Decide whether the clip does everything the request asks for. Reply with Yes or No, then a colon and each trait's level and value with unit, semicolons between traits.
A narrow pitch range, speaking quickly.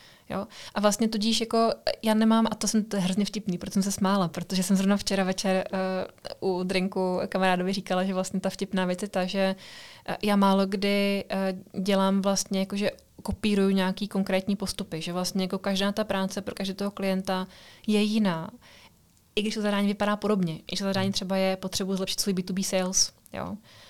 Yes: narrow, 1.3 semitones; fast, 190 wpm